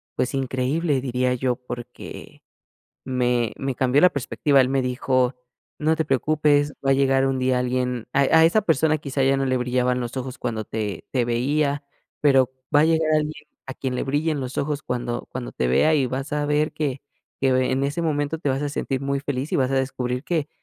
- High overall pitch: No, low, 135 Hz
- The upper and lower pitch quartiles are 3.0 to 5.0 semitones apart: No, narrow, 2.6 semitones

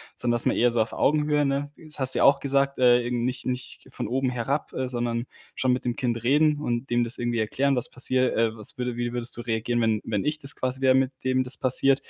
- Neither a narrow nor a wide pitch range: No, narrow, 2.3 semitones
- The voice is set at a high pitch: No, low, 125 Hz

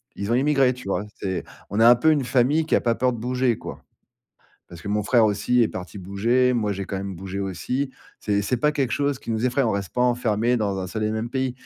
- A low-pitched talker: Yes, low, 115 Hz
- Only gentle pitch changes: No, average, 4.0 semitones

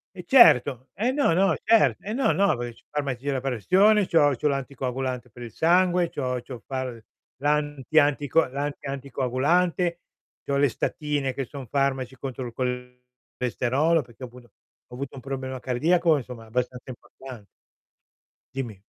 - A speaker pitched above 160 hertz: No, low, 135 Hz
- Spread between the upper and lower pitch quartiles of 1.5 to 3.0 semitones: No, average, 3.8 semitones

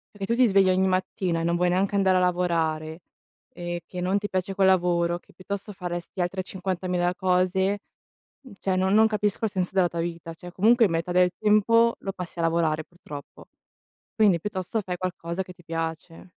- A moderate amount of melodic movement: No, narrow, 2.1 semitones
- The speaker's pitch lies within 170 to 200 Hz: Yes, medium, 185 Hz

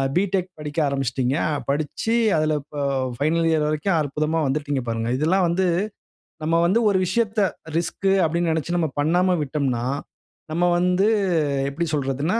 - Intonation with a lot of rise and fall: No, average, 3.7 semitones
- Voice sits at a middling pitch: Yes, medium, 160 Hz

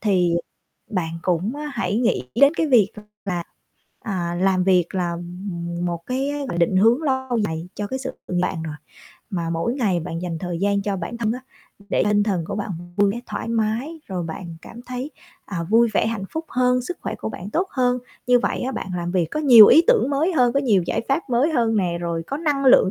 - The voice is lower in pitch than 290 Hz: Yes, high, 205 Hz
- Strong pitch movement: Yes, wide, 6.1 semitones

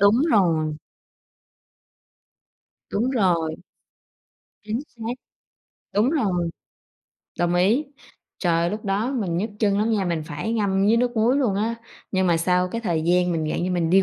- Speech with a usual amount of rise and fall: Yes, average, 4.2 semitones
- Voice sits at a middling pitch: No, high, 195 Hz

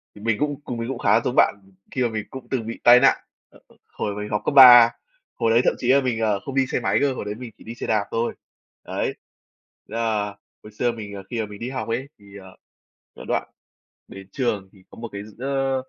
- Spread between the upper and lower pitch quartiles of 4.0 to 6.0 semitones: No, average, 3.5 semitones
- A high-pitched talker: No, low, 115 Hz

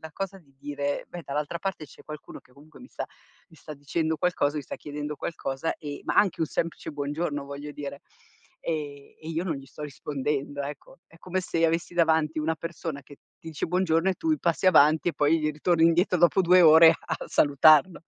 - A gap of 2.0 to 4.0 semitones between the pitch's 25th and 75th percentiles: Yes, average, 2.7 semitones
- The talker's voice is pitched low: No, medium, 155 Hz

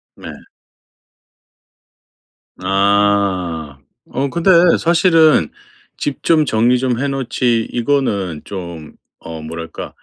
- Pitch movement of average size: No, wide, 7.7 semitones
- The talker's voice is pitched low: Yes, low, 110 Hz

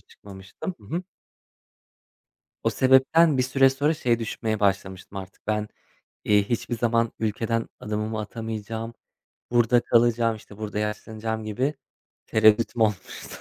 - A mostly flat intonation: Yes, narrow, 2.2 semitones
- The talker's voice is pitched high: No, low, 110 Hz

